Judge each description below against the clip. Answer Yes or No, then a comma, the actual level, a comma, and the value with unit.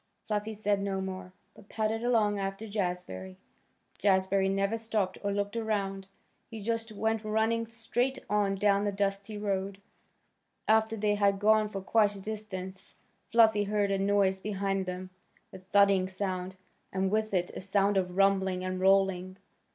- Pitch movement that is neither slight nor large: No, narrow, 1.9 semitones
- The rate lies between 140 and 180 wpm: Yes, average, 155 wpm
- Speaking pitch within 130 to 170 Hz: No, high, 200 Hz